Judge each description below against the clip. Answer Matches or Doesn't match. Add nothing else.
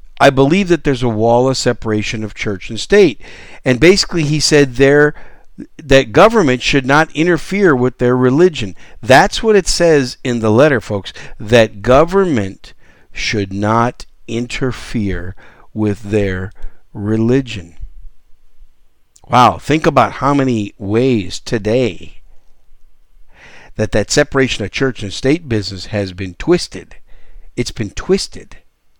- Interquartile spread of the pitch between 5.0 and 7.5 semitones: Matches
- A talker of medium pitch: Doesn't match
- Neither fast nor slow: Doesn't match